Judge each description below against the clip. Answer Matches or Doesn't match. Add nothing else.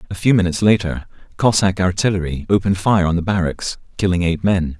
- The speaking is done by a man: Matches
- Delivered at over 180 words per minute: Doesn't match